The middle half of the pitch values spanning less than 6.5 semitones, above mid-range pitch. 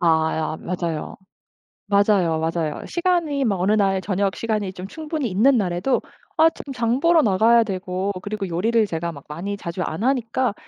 Yes: average, 5.1 semitones; high, 200 Hz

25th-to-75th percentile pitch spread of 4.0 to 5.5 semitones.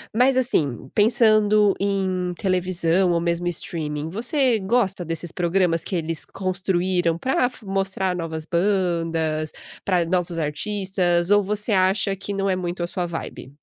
No: average, 2.8 semitones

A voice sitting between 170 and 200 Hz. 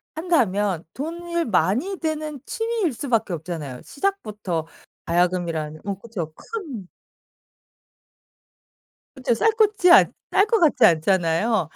No: high, 225 Hz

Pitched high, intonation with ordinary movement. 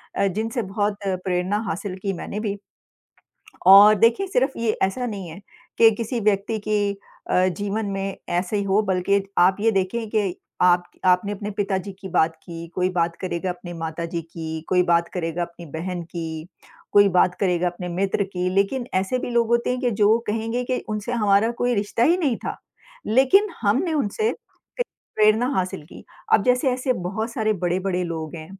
Yes: high, 200 Hz; average, 3.8 semitones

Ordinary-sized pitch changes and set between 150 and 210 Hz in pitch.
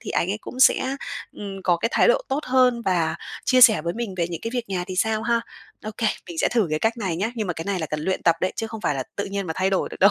Yes: average, 4.6 semitones; high, 200 Hz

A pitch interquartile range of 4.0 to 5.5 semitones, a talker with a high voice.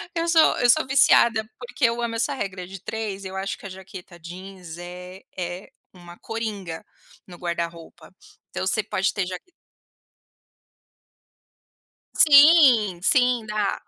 Yes: average, 4.4 semitones; high, 195 Hz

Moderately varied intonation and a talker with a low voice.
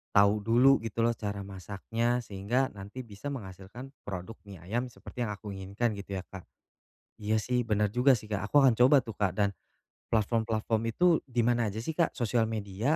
Yes: average, 3.2 semitones; low, 110 Hz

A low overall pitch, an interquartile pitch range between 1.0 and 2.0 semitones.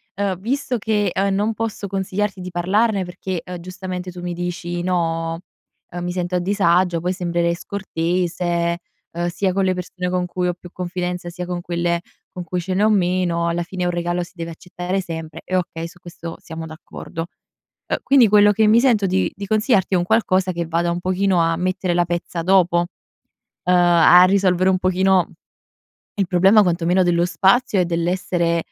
No: medium, 180 Hz; narrow, 1.7 semitones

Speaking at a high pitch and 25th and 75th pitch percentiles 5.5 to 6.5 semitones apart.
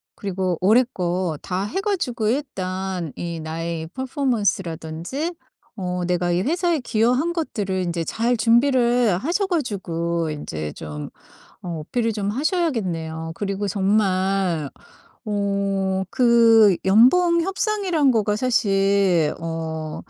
Yes: high, 200 Hz; wide, 6.2 semitones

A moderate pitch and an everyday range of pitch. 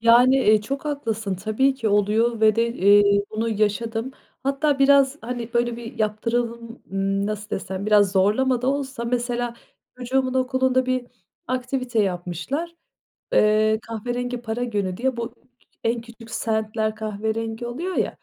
No: high, 230 Hz; average, 3.0 semitones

